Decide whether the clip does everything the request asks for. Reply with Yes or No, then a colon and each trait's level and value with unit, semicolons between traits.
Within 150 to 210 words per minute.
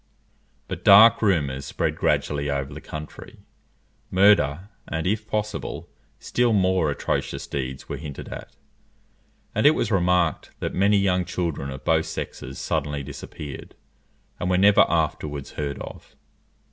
No: slow, 135 wpm